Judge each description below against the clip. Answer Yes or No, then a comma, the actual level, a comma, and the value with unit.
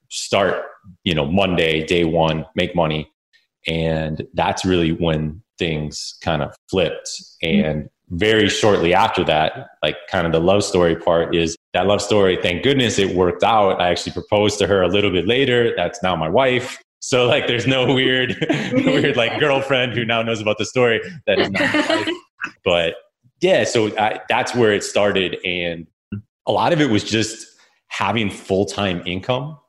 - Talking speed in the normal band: Yes, average, 170 wpm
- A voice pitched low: Yes, low, 100 Hz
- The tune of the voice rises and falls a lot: Yes, wide, 6.6 semitones